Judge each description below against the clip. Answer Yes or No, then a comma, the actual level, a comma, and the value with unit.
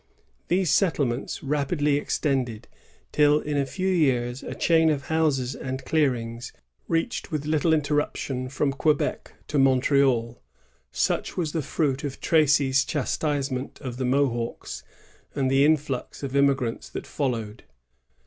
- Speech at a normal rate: No, slow, 130 wpm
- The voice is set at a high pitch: No, medium, 140 Hz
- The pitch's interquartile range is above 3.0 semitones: No, average, 2.7 semitones